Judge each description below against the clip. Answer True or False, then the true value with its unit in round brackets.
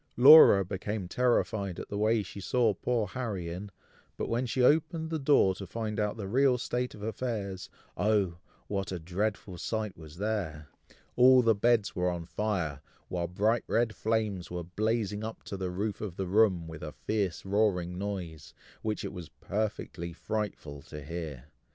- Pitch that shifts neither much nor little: True (3.8 semitones)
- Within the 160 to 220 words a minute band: True (175 wpm)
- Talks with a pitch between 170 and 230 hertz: False (100 Hz)